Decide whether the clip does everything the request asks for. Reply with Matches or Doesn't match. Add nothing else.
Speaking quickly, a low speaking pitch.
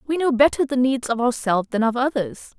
Doesn't match